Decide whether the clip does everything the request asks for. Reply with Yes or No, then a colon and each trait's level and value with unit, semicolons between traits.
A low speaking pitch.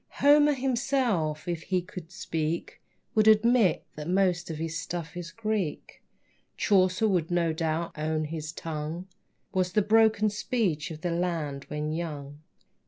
No: medium, 175 Hz